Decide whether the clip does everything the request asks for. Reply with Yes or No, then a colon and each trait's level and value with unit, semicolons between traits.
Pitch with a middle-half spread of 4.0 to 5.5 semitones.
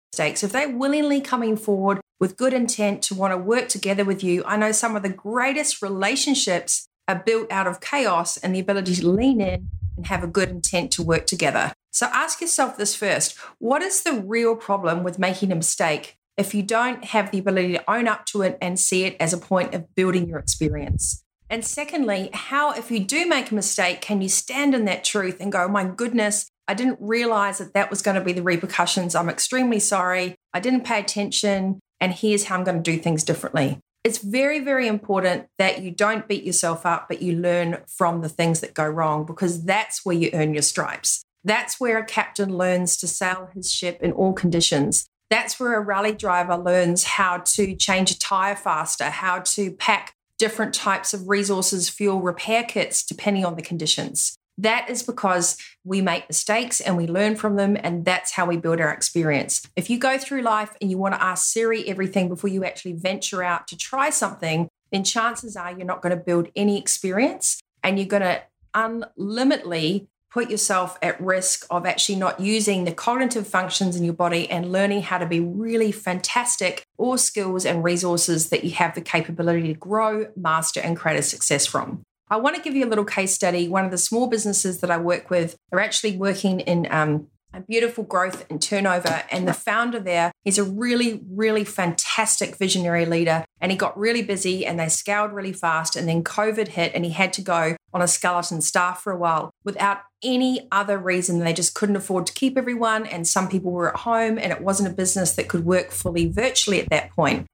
No: average, 3.4 semitones